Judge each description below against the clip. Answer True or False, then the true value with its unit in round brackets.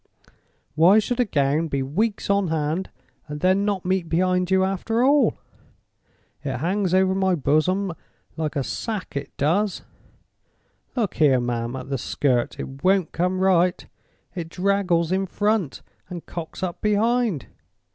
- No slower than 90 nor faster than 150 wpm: True (145 wpm)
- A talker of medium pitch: True (180 Hz)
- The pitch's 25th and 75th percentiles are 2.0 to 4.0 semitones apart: False (4.5 semitones)